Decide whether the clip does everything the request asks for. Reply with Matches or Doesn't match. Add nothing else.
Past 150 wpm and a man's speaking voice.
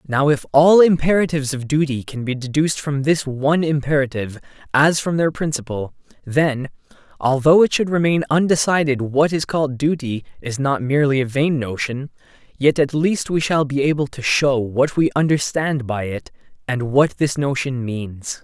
Matches